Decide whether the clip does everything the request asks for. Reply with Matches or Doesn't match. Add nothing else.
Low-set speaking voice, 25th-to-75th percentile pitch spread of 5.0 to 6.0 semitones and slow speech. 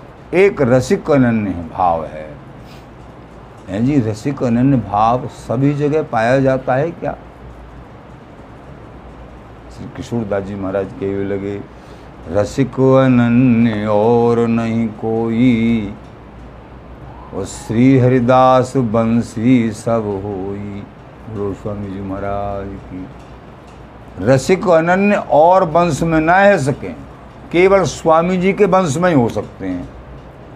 Matches